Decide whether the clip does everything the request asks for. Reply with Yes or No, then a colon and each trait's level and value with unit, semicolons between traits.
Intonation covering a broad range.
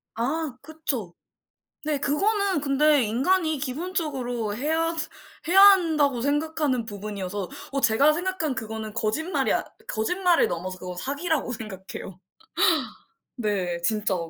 Yes: wide, 6.7 semitones